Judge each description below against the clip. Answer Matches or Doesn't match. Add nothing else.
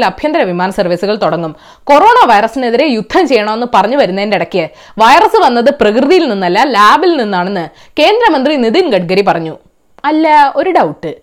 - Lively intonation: Matches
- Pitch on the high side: Matches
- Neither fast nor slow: Doesn't match